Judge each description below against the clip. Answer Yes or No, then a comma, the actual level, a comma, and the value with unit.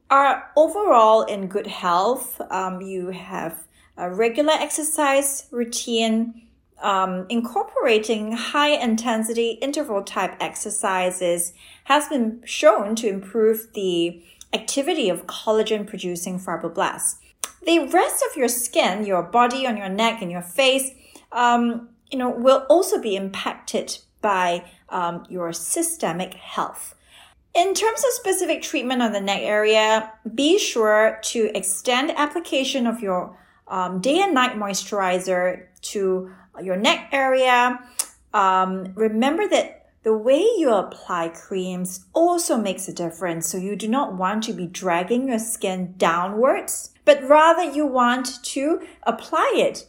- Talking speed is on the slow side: Yes, slow, 130 wpm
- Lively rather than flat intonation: Yes, wide, 6.5 semitones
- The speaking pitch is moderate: No, high, 225 Hz